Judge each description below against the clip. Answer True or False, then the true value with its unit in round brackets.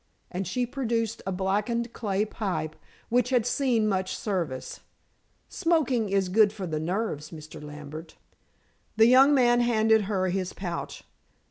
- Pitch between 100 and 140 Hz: False (210 Hz)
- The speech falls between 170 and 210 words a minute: False (140 wpm)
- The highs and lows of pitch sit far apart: False (4.5 semitones)